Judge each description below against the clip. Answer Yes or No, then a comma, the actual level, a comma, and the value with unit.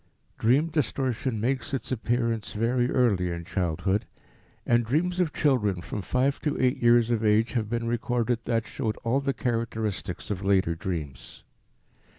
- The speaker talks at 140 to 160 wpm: Yes, average, 155 wpm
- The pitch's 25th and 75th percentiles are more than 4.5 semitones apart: No, average, 3.5 semitones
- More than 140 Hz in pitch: No, low, 115 Hz